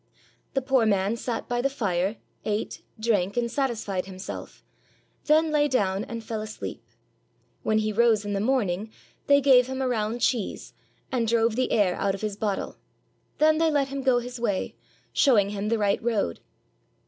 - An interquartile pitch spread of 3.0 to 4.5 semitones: Yes, average, 4.0 semitones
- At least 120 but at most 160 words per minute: No, average, 175 wpm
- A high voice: Yes, high, 230 Hz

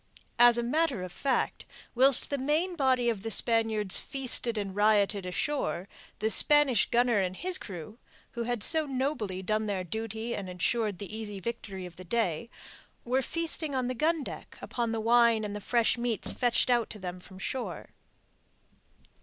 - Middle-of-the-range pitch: No, high, 230 Hz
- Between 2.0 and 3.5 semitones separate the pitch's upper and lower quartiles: No, average, 4.1 semitones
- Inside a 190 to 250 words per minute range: No, average, 175 wpm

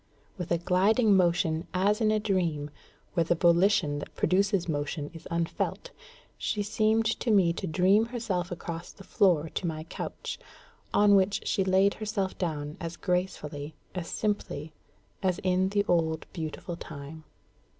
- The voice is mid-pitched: Yes, medium, 180 Hz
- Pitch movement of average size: Yes, average, 3.6 semitones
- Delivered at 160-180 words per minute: No, average, 150 wpm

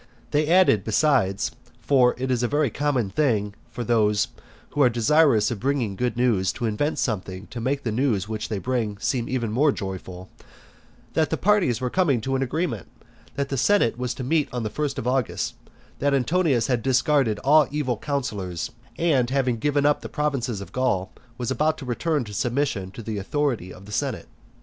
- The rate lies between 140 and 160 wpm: No, average, 190 wpm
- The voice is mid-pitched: No, low, 125 Hz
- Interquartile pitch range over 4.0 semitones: Yes, average, 4.8 semitones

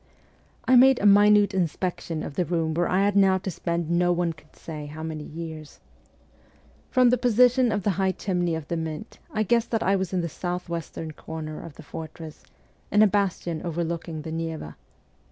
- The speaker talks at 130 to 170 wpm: No, average, 200 wpm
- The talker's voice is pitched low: No, medium, 175 Hz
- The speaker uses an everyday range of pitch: Yes, average, 3.8 semitones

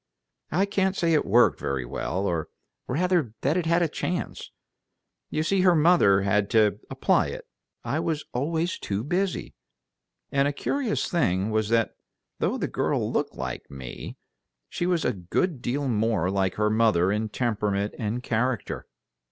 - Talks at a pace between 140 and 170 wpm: Yes, average, 160 wpm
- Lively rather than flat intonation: Yes, wide, 8.6 semitones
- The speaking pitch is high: No, low, 120 Hz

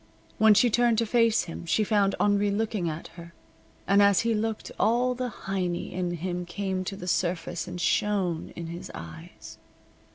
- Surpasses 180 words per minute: No, average, 175 wpm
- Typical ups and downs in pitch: Yes, average, 3.7 semitones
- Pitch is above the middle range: Yes, high, 195 Hz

